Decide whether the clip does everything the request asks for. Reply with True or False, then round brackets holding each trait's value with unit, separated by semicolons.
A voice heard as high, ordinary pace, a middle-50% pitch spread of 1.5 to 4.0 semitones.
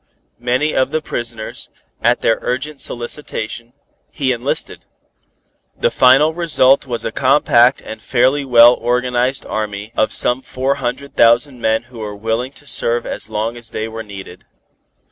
False (120 Hz; 150 wpm; 2.8 semitones)